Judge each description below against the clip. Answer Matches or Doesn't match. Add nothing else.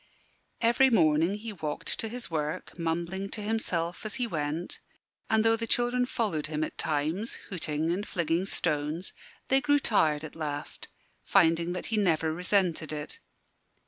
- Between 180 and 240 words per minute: Doesn't match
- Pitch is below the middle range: Doesn't match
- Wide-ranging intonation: Matches